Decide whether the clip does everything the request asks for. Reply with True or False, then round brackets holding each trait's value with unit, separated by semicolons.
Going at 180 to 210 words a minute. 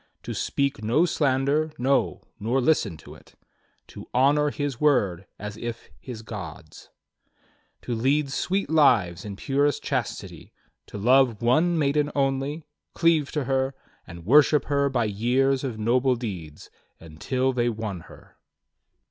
False (140 wpm)